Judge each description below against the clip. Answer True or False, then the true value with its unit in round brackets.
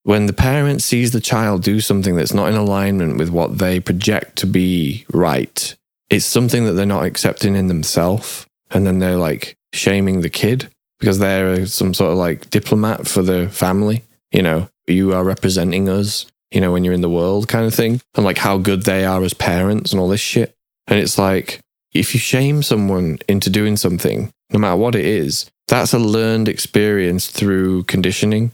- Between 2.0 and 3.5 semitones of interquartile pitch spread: True (2.9 semitones)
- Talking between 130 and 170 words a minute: False (195 wpm)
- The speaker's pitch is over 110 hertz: False (100 Hz)